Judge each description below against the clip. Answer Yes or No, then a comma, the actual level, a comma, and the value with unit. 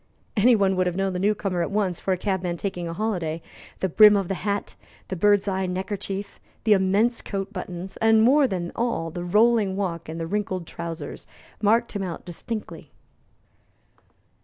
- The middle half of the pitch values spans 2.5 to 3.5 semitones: Yes, average, 2.8 semitones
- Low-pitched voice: No, high, 195 Hz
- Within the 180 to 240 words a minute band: Yes, average, 185 wpm